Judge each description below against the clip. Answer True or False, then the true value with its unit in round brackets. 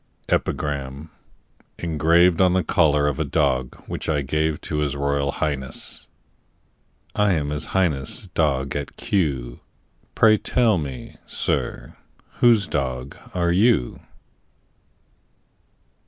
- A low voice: True (75 Hz)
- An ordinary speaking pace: False (110 wpm)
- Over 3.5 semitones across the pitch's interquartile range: True (3.9 semitones)